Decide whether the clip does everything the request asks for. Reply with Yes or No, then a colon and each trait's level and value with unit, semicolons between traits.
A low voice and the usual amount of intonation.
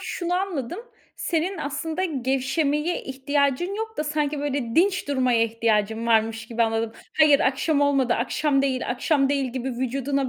No: very high, 275 Hz; average, 3.7 semitones